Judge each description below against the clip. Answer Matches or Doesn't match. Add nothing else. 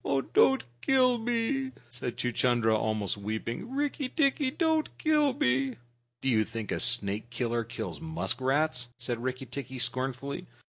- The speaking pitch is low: Matches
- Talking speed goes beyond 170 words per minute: Doesn't match